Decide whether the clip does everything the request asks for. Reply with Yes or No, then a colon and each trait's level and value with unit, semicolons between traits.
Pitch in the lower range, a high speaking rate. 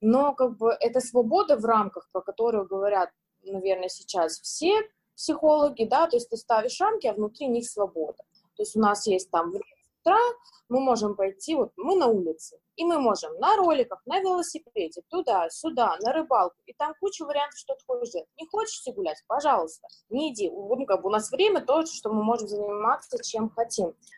No: very high, 250 Hz; fast, 180 wpm